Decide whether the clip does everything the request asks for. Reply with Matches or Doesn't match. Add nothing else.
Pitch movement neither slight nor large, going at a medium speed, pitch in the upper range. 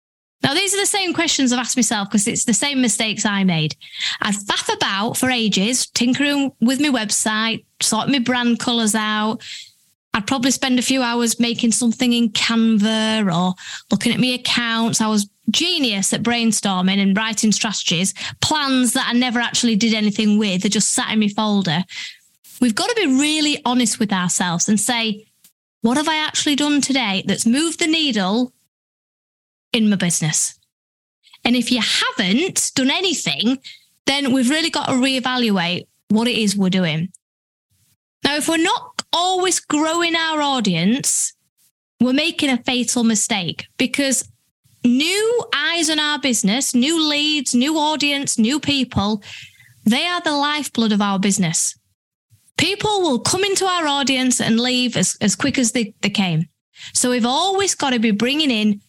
Matches